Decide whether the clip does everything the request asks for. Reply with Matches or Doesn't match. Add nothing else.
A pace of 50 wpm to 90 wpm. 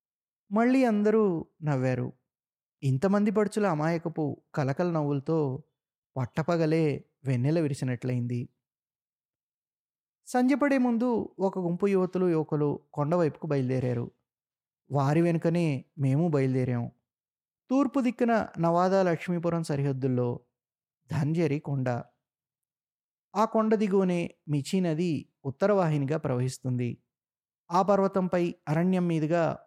Matches